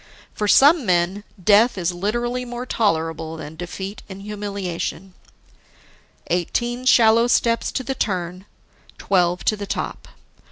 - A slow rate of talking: Yes, slow, 125 wpm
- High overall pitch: Yes, high, 200 Hz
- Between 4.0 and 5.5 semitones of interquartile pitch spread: Yes, average, 5.0 semitones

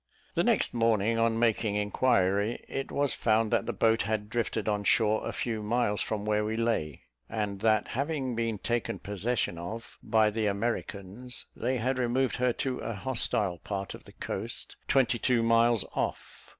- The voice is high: No, low, 115 Hz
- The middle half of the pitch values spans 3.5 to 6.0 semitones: No, narrow, 2.5 semitones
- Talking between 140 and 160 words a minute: No, average, 175 wpm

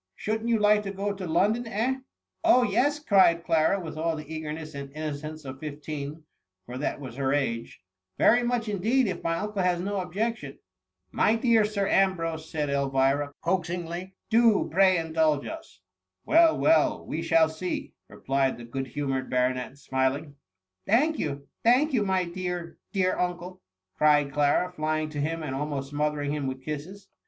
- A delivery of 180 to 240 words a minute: Yes, average, 190 wpm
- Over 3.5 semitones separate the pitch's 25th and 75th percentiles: Yes, wide, 5.6 semitones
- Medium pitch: Yes, medium, 165 Hz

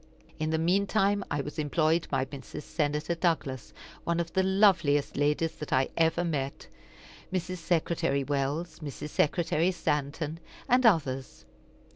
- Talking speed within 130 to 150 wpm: Yes, average, 140 wpm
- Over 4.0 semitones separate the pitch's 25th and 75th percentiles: No, average, 3.1 semitones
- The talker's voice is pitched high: No, medium, 160 Hz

